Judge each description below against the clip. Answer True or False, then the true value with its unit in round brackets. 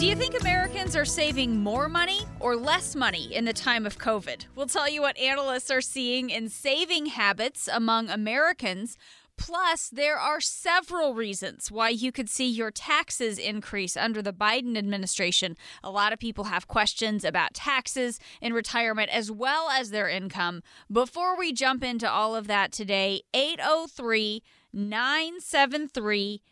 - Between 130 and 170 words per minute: True (155 wpm)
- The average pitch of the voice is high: True (235 Hz)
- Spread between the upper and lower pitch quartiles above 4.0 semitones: True (5.1 semitones)